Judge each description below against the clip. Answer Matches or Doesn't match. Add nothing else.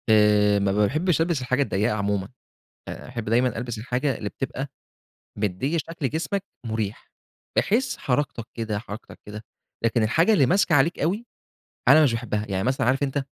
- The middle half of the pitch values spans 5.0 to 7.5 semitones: Matches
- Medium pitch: Doesn't match